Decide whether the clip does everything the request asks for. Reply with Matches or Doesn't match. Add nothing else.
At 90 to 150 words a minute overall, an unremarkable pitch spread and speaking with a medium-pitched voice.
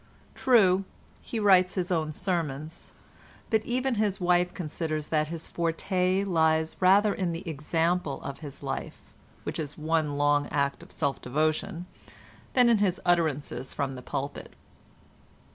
Matches